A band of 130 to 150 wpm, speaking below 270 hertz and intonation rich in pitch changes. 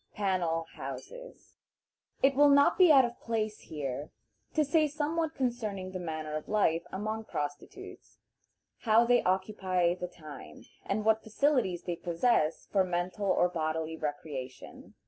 Yes: average, 140 wpm; high, 190 Hz; wide, 6.7 semitones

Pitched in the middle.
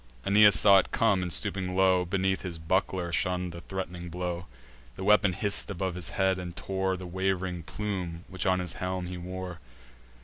No: very low, 95 Hz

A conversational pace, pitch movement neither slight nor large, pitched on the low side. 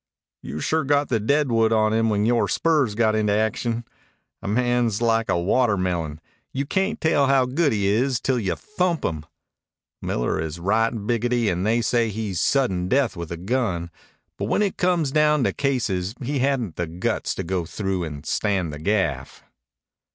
No: average, 180 wpm; wide, 5.9 semitones; low, 110 Hz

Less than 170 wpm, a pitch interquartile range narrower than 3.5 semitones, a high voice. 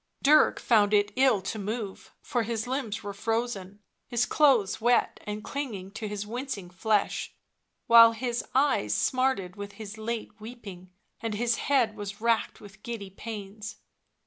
Yes: average, 150 wpm; average, 2.9 semitones; high, 220 Hz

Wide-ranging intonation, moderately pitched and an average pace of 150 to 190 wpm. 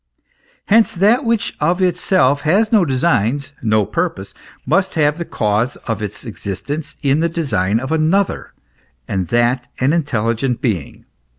No: wide, 7.0 semitones; medium, 145 Hz; average, 140 wpm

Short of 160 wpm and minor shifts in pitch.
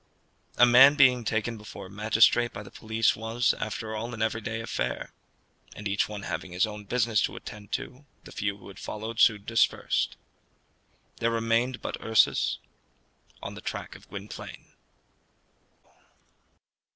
Yes: average, 150 wpm; narrow, 1.9 semitones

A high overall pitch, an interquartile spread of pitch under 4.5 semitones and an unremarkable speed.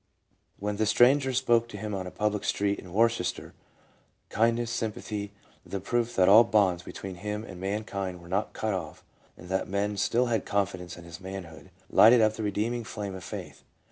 No: low, 105 Hz; average, 3.0 semitones; average, 185 wpm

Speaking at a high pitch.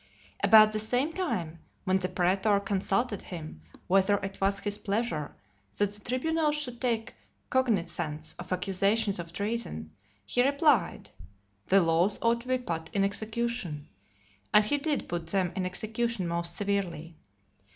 Yes: high, 200 Hz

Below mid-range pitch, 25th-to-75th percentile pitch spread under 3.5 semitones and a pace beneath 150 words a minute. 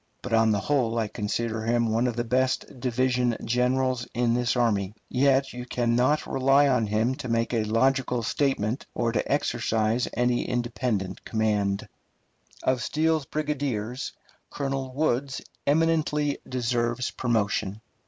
Yes: low, 125 Hz; average, 2.7 semitones; average, 140 wpm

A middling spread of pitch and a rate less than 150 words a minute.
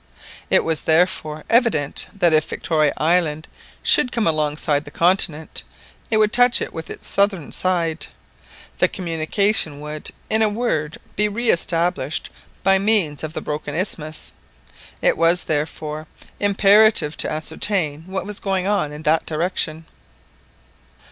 Yes: average, 4.5 semitones; average, 140 wpm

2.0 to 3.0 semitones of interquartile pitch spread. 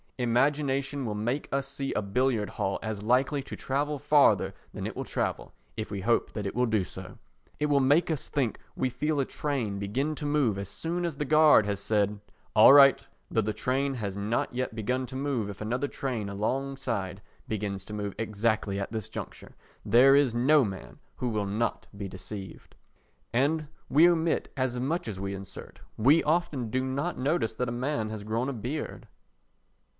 No: average, 4.8 semitones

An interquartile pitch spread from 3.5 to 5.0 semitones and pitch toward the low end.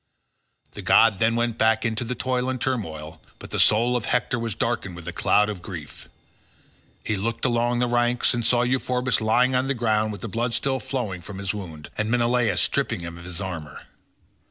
Yes: average, 4.0 semitones; low, 115 Hz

